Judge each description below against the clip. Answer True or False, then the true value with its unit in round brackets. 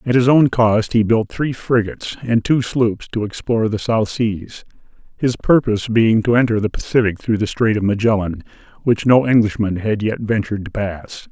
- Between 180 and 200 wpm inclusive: True (190 wpm)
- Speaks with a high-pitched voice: False (110 Hz)